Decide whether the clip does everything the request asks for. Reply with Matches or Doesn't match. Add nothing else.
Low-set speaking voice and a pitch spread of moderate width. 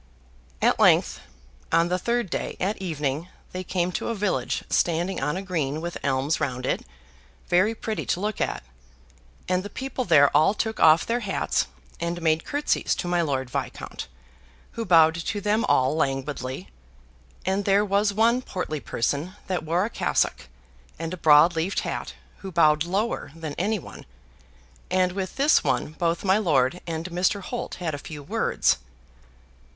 Doesn't match